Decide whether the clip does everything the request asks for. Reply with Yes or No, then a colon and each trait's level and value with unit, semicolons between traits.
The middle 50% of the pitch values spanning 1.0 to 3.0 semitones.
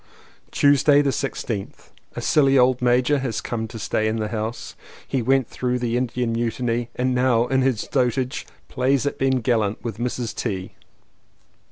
Yes: narrow, 2.4 semitones